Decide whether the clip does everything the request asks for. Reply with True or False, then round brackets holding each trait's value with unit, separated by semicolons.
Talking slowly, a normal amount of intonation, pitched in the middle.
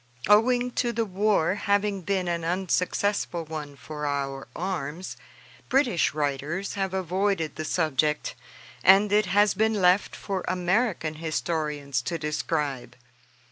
True (125 wpm; 4.7 semitones; 180 Hz)